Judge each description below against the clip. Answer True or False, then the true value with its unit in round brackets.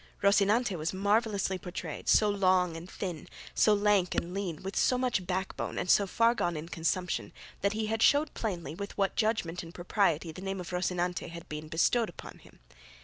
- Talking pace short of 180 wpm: False (185 wpm)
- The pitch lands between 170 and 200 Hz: True (185 Hz)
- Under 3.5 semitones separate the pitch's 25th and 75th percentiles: True (3.1 semitones)